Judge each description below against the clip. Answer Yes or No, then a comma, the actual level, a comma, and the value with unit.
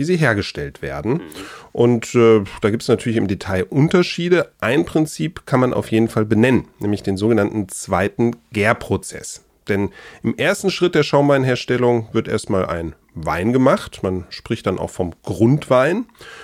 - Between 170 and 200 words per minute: No, average, 155 wpm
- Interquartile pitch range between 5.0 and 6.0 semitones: Yes, wide, 5.5 semitones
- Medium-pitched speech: No, low, 115 Hz